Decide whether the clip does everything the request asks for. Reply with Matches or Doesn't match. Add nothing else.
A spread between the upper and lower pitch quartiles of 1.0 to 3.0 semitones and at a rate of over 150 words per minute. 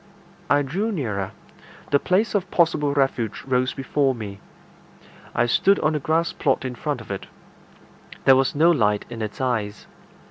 Doesn't match